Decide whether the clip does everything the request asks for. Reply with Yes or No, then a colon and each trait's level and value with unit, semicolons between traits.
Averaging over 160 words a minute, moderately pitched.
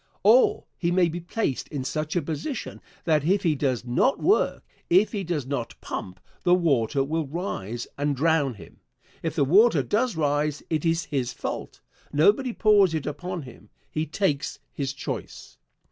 Yes: average, 170 wpm; medium, 155 Hz